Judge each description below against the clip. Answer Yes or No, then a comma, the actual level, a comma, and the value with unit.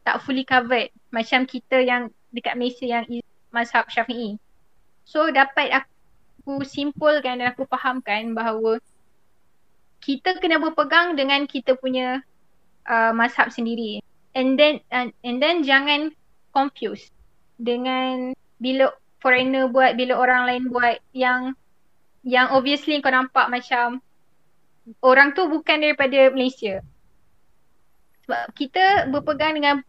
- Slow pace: No, average, 115 wpm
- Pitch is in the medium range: No, very high, 255 Hz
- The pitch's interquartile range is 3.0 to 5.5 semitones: No, narrow, 2.4 semitones